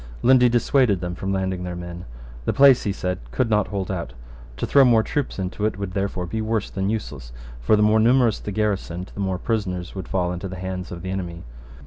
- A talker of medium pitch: No, very low, 95 Hz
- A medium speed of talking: No, fast, 225 wpm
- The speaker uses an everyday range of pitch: Yes, average, 3.3 semitones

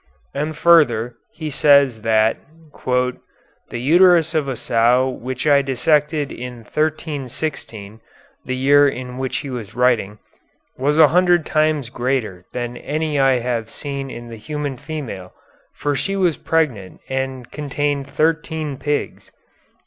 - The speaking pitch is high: No, low, 135 Hz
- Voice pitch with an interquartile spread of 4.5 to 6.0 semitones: No, average, 3.8 semitones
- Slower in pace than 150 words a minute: Yes, slow, 135 wpm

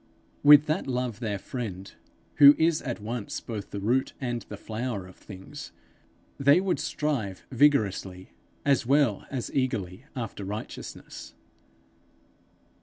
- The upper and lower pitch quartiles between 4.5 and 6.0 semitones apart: Yes, wide, 5.6 semitones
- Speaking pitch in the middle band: No, low, 120 Hz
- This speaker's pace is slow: Yes, slow, 130 wpm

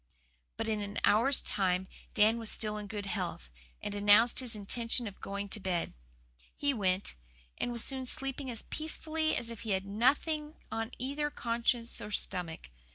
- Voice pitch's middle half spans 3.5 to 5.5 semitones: Yes, average, 4.0 semitones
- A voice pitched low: No, high, 225 Hz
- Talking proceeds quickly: No, average, 170 wpm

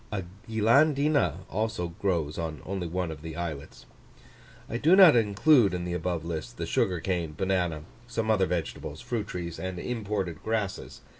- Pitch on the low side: Yes, very low, 95 Hz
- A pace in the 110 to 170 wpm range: Yes, average, 160 wpm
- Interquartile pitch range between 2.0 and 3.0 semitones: No, average, 4.6 semitones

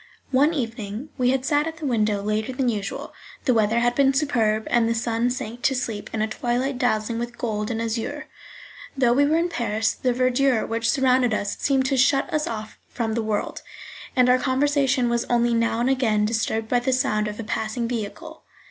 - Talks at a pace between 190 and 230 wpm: Yes, fast, 205 wpm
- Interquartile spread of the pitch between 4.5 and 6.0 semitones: No, average, 3.1 semitones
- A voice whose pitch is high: Yes, high, 240 Hz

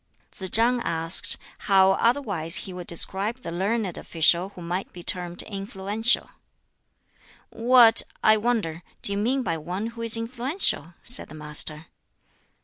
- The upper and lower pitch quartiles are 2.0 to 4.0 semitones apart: No, average, 5.0 semitones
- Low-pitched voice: No, high, 195 Hz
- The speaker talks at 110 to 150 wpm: Yes, average, 140 wpm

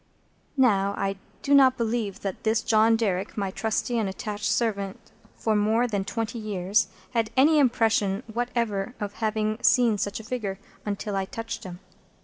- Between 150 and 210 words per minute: Yes, average, 160 wpm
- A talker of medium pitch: No, high, 215 Hz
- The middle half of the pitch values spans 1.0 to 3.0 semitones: Yes, narrow, 2.6 semitones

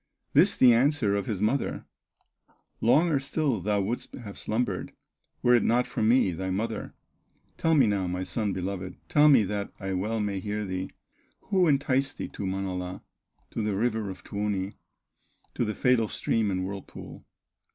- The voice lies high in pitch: No, low, 105 Hz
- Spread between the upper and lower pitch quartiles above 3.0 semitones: Yes, average, 4.2 semitones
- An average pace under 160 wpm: No, average, 165 wpm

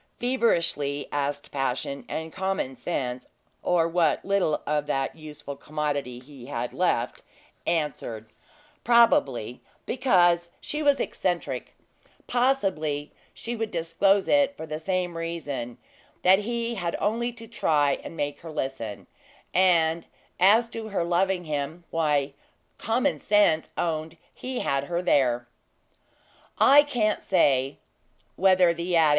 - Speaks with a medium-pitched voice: Yes, medium, 165 Hz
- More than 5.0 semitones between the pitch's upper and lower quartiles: Yes, wide, 5.6 semitones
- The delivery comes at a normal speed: No, slow, 125 wpm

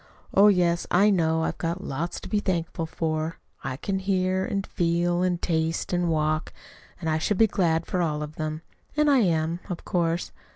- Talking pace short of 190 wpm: No, average, 195 wpm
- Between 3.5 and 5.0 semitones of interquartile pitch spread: No, narrow, 2.5 semitones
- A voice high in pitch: No, medium, 170 Hz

